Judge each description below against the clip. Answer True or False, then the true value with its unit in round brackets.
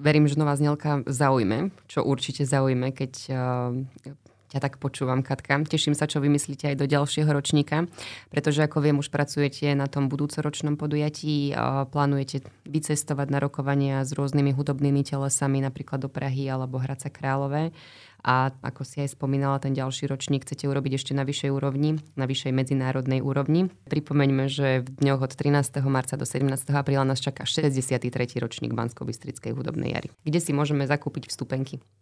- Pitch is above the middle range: False (140 Hz)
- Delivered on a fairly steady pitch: True (1.5 semitones)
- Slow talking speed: False (155 wpm)